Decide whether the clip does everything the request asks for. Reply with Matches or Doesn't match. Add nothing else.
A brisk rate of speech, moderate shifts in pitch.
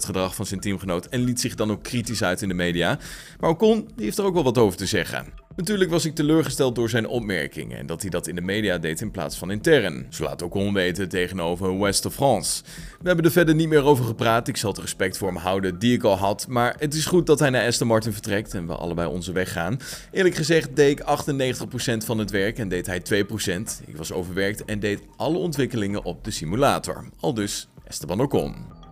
Doesn't match